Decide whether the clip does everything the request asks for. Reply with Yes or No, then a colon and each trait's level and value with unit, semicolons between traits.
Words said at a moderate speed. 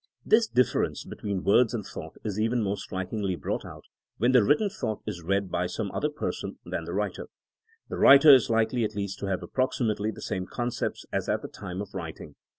No: fast, 210 wpm